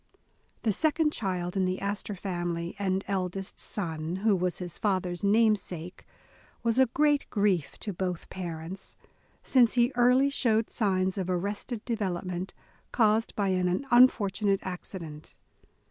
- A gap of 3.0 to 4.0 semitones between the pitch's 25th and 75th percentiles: Yes, average, 3.6 semitones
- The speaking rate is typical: No, slow, 130 wpm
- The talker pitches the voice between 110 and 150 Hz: No, high, 195 Hz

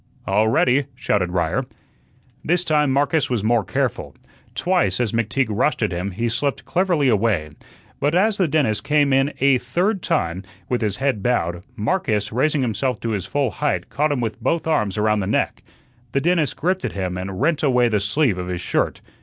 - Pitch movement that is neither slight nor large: No, wide, 6.0 semitones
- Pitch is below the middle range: Yes, low, 125 Hz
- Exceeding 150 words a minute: Yes, average, 190 wpm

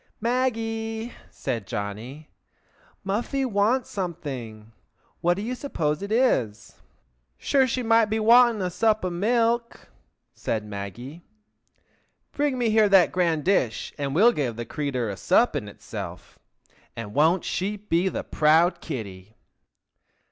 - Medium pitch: Yes, medium, 180 Hz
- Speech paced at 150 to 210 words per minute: No, slow, 135 wpm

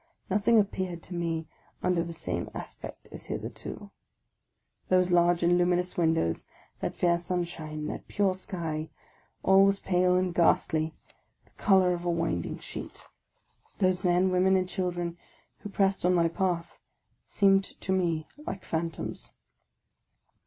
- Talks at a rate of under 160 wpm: Yes, average, 145 wpm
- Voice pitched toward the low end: No, medium, 180 Hz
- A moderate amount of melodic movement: No, narrow, 1.8 semitones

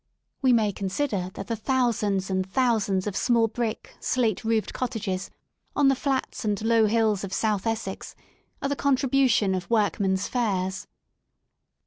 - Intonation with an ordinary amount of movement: Yes, average, 4.0 semitones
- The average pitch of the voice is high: Yes, high, 220 Hz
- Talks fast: No, average, 150 wpm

